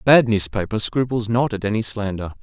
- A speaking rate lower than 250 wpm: Yes, average, 200 wpm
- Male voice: Yes, male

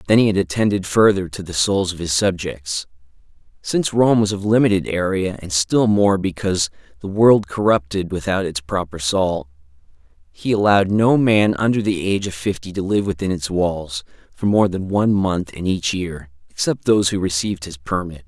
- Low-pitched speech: Yes, very low, 95 Hz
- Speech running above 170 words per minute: Yes, average, 185 wpm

